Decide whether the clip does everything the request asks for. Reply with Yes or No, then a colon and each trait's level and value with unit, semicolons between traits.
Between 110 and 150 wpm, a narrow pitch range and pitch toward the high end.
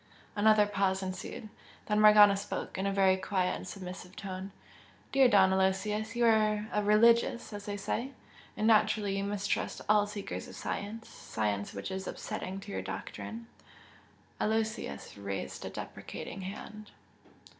Yes: average, 145 wpm; narrow, 2.1 semitones; high, 205 Hz